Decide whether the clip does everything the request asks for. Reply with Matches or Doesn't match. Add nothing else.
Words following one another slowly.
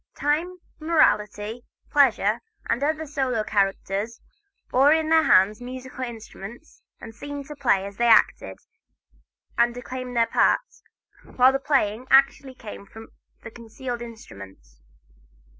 Matches